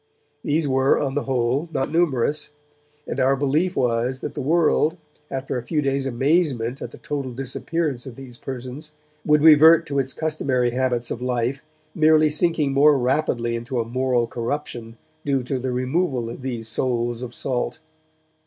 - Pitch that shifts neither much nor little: Yes, average, 3.5 semitones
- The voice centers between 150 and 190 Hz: No, low, 135 Hz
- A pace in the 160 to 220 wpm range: Yes, average, 165 wpm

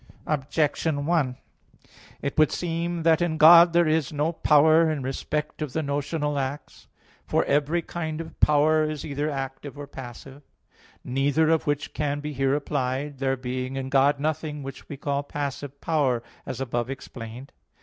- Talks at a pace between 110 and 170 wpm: Yes, average, 165 wpm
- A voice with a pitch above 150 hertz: No, medium, 145 Hz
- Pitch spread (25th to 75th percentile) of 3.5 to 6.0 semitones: No, narrow, 2.5 semitones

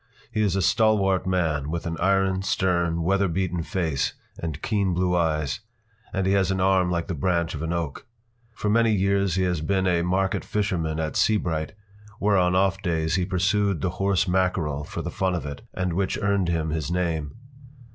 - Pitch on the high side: No, very low, 90 Hz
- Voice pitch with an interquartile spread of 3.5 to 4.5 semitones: No, average, 2.7 semitones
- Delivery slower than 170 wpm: No, average, 195 wpm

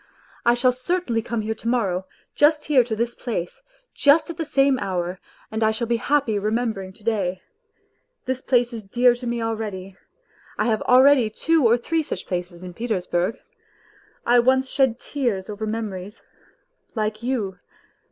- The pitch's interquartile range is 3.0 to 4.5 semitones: Yes, average, 3.8 semitones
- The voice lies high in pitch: Yes, high, 230 Hz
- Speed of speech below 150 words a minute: No, average, 180 wpm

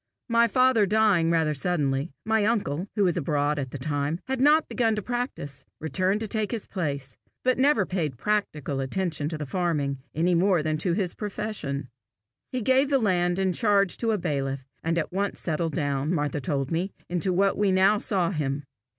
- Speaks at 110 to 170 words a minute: No, average, 195 wpm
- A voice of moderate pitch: Yes, medium, 175 Hz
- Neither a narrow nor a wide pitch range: No, wide, 6.2 semitones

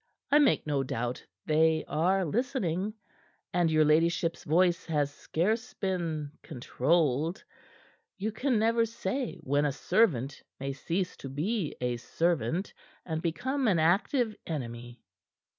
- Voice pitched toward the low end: No, medium, 165 Hz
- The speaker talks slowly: Yes, slow, 125 wpm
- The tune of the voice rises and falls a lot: Yes, wide, 5.9 semitones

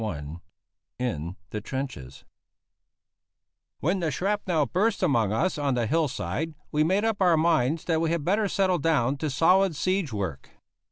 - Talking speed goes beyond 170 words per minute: No, average, 160 wpm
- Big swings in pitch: Yes, wide, 6.8 semitones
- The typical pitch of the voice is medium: Yes, medium, 155 Hz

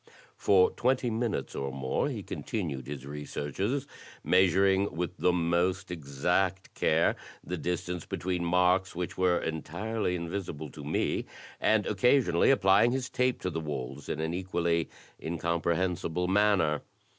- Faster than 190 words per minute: No, slow, 135 wpm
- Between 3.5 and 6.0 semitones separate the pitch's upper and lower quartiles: No, average, 3.1 semitones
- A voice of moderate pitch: No, very low, 90 Hz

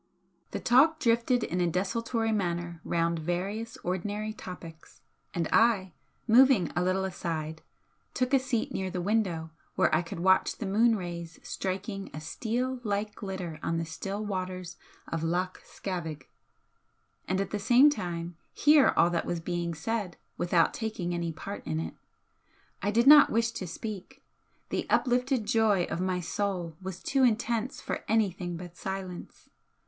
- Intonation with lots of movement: No, average, 4.5 semitones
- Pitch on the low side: No, high, 190 Hz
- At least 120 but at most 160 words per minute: Yes, average, 155 wpm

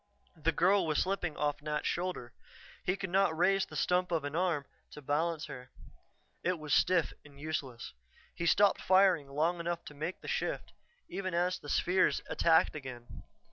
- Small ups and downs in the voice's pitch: No, average, 3.6 semitones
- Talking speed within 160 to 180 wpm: Yes, average, 175 wpm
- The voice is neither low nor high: Yes, medium, 170 Hz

